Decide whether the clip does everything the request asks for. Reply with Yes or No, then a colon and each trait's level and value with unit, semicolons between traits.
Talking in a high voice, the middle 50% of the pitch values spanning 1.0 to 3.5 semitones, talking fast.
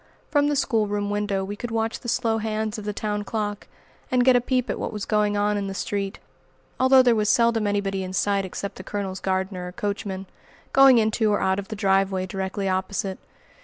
Yes: high, 205 Hz; narrow, 2.4 semitones; fast, 210 wpm